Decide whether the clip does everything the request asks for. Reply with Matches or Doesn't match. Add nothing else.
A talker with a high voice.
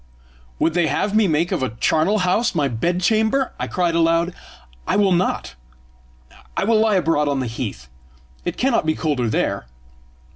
Doesn't match